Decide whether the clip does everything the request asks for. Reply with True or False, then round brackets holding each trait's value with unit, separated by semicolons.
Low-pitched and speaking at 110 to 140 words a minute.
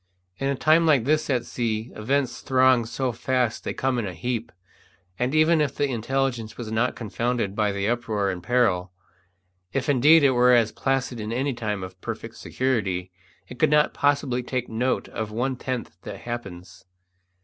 False (125 Hz; 180 wpm)